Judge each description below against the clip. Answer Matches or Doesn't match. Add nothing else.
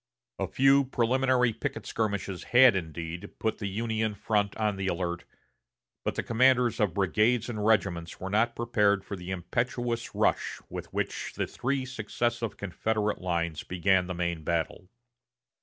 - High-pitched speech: Doesn't match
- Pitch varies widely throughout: Doesn't match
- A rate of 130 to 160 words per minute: Matches